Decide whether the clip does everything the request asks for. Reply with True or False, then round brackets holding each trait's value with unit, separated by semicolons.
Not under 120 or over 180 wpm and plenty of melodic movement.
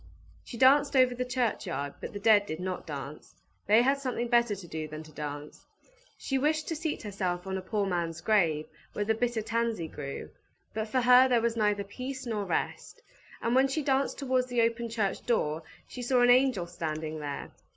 False (200 wpm; 6.3 semitones)